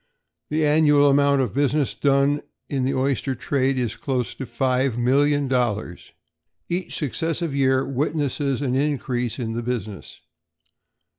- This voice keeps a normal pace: No, slow, 130 wpm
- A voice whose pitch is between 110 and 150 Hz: Yes, low, 135 Hz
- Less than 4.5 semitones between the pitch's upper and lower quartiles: Yes, narrow, 2.4 semitones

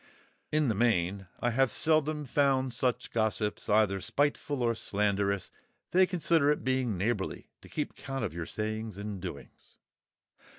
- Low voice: Yes, low, 115 Hz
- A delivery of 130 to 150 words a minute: Yes, average, 145 wpm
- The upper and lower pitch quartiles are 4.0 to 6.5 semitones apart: Yes, average, 5.3 semitones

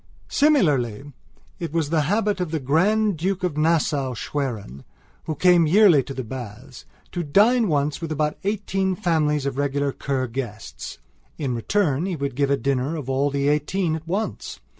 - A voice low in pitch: No, medium, 150 Hz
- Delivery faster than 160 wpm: Yes, average, 170 wpm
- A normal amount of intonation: Yes, average, 4.8 semitones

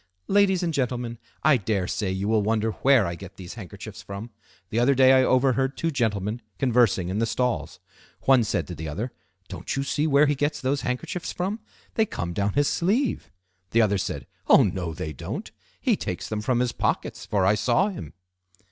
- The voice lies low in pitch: Yes, low, 120 Hz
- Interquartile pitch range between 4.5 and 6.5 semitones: Yes, wide, 5.6 semitones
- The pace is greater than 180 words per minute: Yes, average, 200 wpm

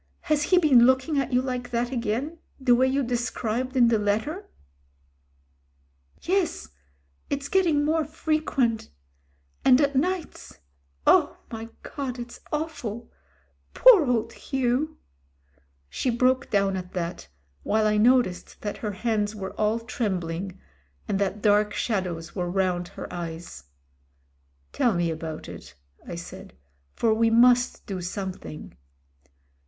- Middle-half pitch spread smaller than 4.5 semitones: No, average, 5.3 semitones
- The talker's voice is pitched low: No, high, 230 Hz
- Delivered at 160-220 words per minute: No, slow, 135 wpm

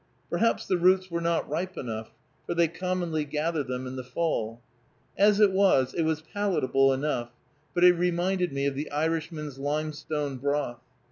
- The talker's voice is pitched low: No, medium, 155 Hz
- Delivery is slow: No, average, 165 wpm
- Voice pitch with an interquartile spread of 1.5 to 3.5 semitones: No, average, 4.3 semitones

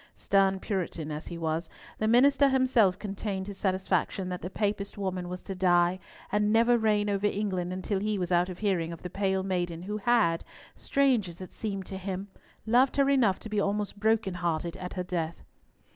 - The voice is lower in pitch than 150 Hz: No, high, 195 Hz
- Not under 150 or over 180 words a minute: No, average, 190 wpm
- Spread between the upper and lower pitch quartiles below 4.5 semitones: Yes, average, 2.8 semitones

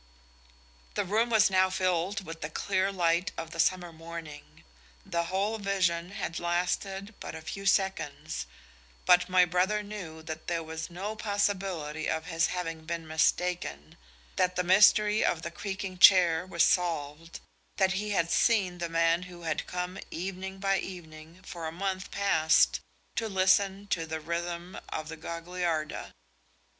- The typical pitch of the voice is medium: Yes, medium, 180 Hz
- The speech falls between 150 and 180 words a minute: Yes, average, 155 wpm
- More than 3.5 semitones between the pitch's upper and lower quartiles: No, average, 2.8 semitones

